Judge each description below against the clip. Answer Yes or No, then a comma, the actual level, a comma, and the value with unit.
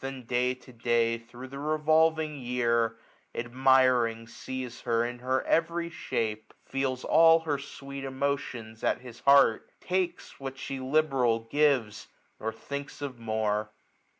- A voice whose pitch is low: Yes, low, 130 Hz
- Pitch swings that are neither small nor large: Yes, average, 3.3 semitones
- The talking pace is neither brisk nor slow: Yes, average, 150 wpm